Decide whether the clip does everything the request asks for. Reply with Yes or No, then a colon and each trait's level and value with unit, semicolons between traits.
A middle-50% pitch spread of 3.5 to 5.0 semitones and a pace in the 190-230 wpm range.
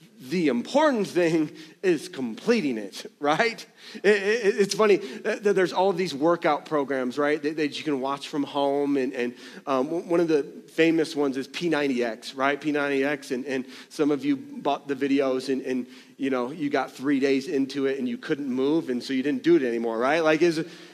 Yes: average, 4.4 semitones; average, 200 wpm